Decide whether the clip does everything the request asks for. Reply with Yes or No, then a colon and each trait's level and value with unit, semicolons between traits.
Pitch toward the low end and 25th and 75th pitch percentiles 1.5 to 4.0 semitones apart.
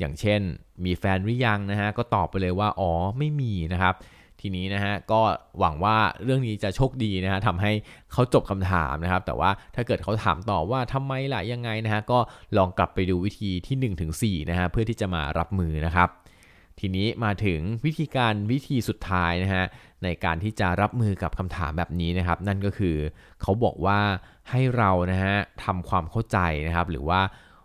Yes: very low, 95 Hz; average, 3.6 semitones